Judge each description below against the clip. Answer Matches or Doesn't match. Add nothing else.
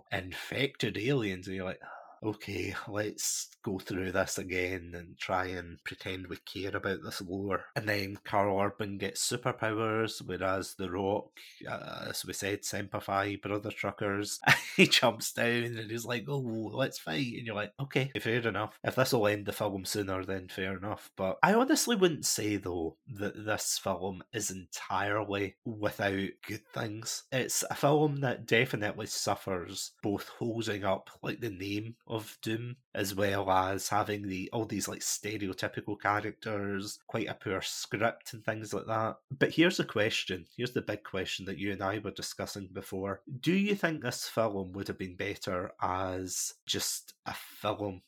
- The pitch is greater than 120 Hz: Doesn't match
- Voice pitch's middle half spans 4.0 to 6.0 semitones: Doesn't match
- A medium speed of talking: Matches